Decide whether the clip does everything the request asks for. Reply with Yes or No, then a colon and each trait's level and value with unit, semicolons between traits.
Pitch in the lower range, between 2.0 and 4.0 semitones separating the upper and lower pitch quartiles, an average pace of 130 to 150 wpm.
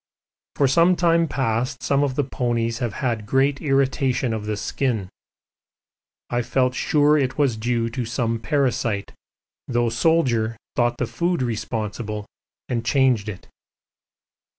Yes: low, 125 Hz; average, 3.3 semitones; average, 140 wpm